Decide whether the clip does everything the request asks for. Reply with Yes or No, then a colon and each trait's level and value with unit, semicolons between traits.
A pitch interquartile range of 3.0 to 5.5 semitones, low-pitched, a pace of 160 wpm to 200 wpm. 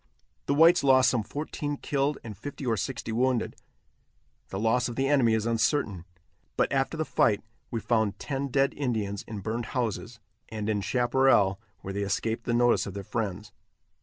Yes: average, 3.9 semitones; low, 120 Hz; average, 175 wpm